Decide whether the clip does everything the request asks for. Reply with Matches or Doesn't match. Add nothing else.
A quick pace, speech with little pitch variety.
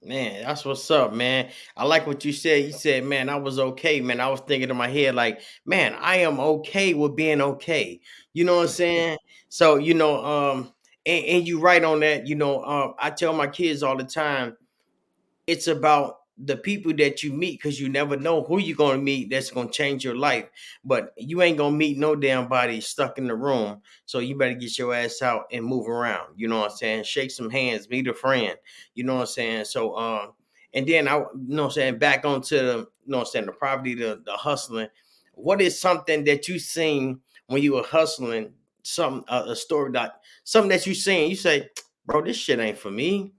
Doesn't match